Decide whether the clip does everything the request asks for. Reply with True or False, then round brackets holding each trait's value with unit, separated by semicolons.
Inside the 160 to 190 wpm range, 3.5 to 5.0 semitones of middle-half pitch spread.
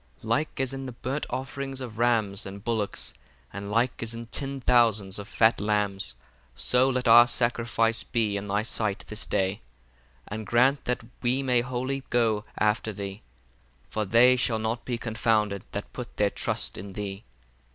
False (170 wpm; 3.1 semitones)